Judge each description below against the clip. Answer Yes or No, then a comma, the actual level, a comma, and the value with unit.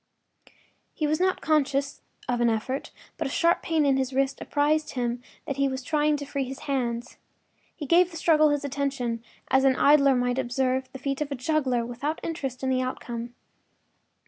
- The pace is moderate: Yes, average, 195 wpm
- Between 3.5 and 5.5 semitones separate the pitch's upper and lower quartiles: No, average, 2.8 semitones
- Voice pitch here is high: Yes, very high, 270 Hz